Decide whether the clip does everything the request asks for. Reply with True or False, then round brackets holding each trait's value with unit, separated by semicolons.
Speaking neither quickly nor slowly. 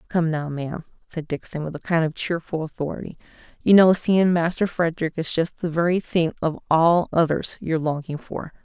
True (190 wpm)